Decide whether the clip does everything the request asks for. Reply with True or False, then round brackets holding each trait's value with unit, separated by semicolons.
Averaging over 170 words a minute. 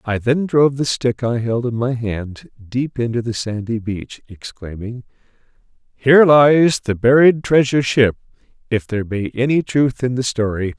False (165 wpm)